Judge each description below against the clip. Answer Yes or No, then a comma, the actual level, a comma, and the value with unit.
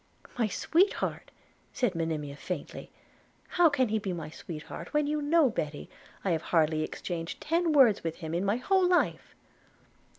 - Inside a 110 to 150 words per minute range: No, average, 160 wpm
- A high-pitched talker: Yes, high, 200 Hz